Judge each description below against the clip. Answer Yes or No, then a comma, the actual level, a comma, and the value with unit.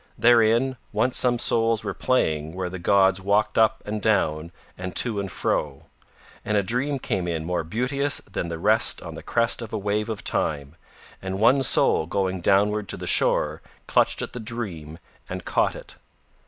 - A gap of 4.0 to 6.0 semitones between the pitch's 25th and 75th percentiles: Yes, average, 4.5 semitones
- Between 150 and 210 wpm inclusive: Yes, average, 180 wpm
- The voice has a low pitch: Yes, low, 100 Hz